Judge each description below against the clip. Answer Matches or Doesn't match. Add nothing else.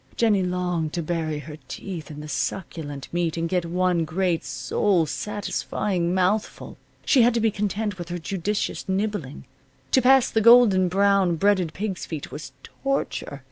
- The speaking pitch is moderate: Matches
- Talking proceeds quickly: Doesn't match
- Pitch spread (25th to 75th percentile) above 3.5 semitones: Matches